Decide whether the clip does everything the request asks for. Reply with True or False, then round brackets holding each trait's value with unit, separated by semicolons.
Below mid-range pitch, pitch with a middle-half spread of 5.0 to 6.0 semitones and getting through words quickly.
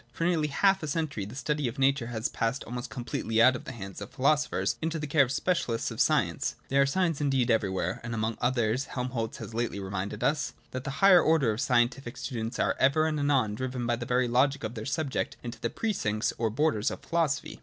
False (130 Hz; 4.1 semitones; 240 wpm)